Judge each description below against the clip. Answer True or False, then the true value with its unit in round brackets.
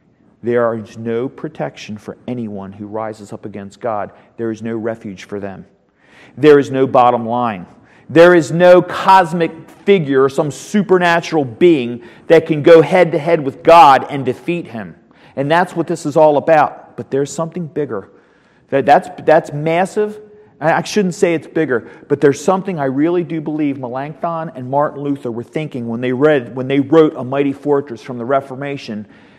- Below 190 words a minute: True (170 wpm)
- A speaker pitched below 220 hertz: True (140 Hz)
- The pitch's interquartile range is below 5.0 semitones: False (5.3 semitones)